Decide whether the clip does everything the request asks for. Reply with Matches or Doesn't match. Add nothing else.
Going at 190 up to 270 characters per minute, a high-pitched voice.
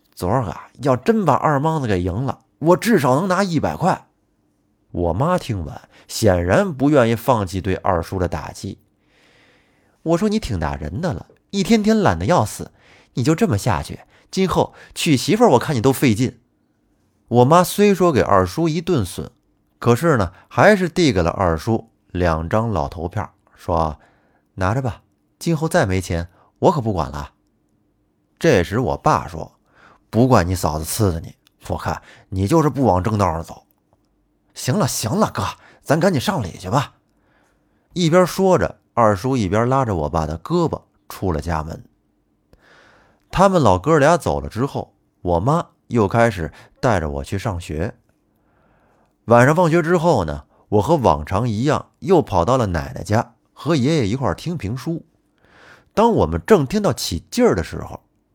Doesn't match